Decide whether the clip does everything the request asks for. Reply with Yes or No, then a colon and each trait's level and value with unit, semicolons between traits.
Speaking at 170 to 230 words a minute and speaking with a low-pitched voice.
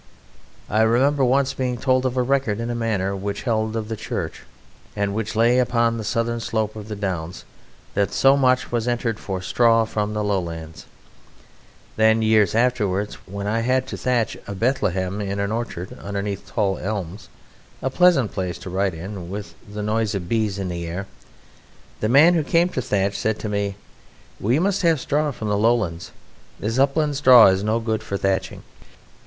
Yes: average, 185 wpm; low, 110 Hz